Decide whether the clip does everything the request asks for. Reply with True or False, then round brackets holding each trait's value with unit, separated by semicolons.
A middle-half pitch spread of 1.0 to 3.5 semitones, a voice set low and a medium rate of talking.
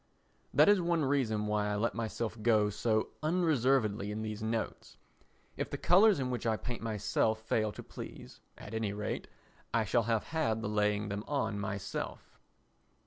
True (2.9 semitones; 110 Hz; 170 wpm)